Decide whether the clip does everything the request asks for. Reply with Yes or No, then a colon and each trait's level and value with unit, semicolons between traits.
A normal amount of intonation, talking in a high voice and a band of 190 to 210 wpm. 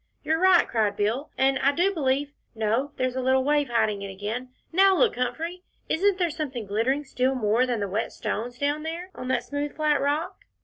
Yes: average, 4.6 semitones; very high, 265 Hz; fast, 205 wpm